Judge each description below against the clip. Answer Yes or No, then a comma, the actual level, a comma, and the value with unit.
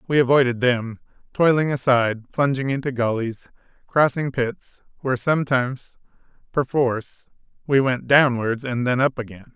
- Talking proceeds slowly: Yes, slow, 125 wpm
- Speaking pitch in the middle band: No, low, 130 Hz